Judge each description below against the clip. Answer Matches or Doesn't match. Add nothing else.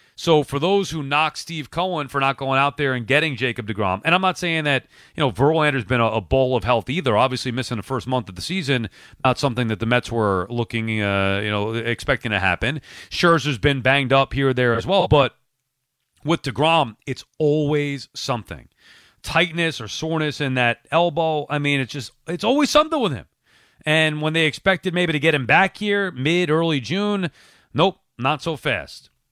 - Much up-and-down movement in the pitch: Doesn't match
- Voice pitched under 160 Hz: Matches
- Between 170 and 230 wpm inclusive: Matches